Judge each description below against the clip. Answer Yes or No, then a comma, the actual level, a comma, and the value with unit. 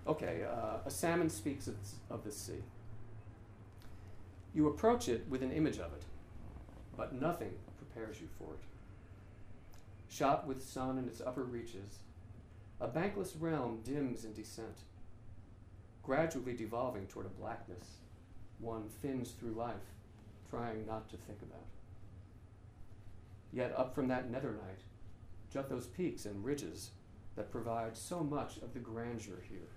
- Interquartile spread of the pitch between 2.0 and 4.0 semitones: Yes, average, 3.5 semitones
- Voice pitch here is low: Yes, low, 110 Hz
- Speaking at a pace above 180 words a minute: No, slow, 135 wpm